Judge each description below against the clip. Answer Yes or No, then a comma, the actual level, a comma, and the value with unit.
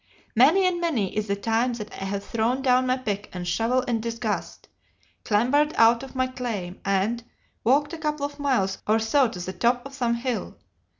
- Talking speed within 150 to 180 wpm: No, average, 195 wpm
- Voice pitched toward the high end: Yes, high, 235 Hz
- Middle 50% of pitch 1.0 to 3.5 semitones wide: No, average, 3.9 semitones